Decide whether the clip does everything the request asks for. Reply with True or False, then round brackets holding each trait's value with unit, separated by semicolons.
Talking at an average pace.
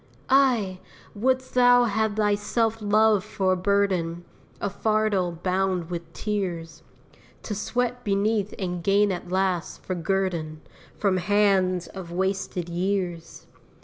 False (125 wpm)